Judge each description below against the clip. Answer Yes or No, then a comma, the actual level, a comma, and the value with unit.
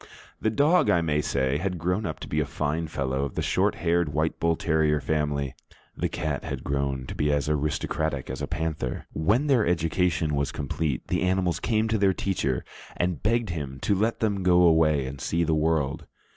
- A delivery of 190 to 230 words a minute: Yes, average, 200 wpm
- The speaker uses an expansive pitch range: No, average, 4.0 semitones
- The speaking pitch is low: Yes, very low, 80 Hz